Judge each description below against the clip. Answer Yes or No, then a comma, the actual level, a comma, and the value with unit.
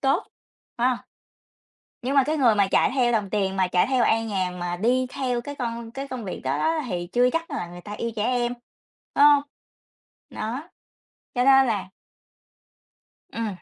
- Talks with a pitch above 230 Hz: Yes, high, 240 Hz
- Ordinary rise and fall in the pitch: Yes, average, 4.6 semitones